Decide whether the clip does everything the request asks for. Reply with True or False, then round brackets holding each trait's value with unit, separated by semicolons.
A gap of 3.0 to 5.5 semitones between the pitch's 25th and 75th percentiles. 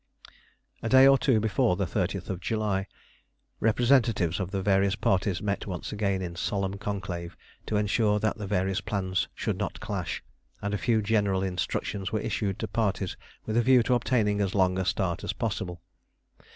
False (2.6 semitones)